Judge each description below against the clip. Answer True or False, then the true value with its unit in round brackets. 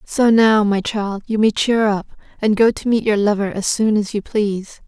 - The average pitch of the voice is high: True (210 Hz)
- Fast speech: True (235 wpm)